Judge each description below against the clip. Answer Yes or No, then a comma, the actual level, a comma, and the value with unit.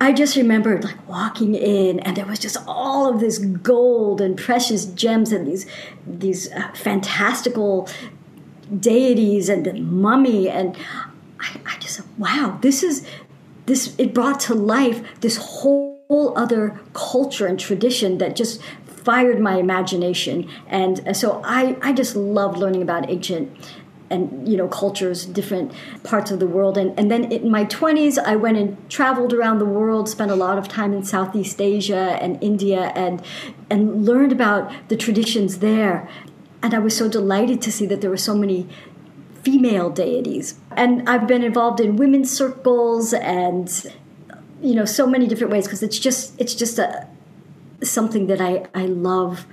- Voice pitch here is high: Yes, high, 210 Hz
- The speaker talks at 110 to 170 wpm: Yes, average, 165 wpm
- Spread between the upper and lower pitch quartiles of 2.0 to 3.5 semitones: No, average, 4.1 semitones